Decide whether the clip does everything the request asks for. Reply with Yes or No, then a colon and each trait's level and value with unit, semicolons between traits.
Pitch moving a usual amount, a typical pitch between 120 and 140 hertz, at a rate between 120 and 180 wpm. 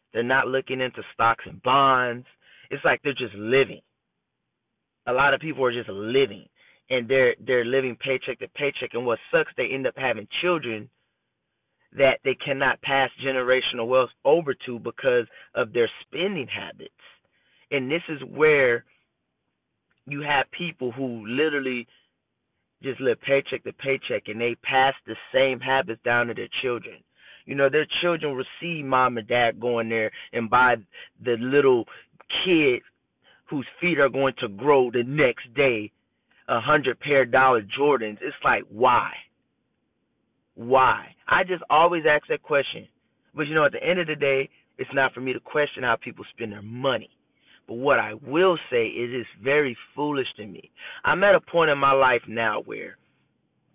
Yes: average, 3.6 semitones; low, 135 Hz; average, 170 wpm